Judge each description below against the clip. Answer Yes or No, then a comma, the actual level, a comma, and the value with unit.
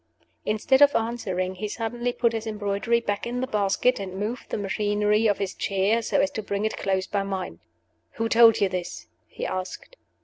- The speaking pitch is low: No, high, 210 Hz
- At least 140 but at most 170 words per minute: No, average, 195 wpm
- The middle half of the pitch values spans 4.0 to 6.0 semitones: No, average, 2.8 semitones